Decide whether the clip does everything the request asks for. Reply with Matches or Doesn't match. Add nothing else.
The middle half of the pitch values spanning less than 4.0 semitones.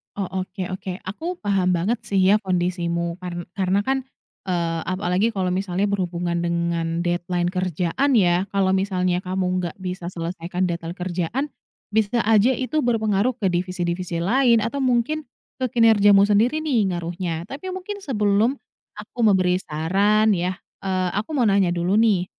Matches